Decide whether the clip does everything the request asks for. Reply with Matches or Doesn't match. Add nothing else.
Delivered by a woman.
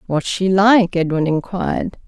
Matches